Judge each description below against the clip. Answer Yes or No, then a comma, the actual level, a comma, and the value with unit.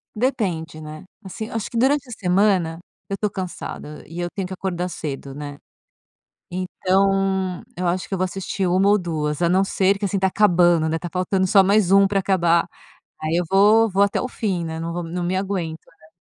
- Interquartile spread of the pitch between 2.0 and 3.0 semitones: Yes, narrow, 2.6 semitones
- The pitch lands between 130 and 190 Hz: Yes, medium, 185 Hz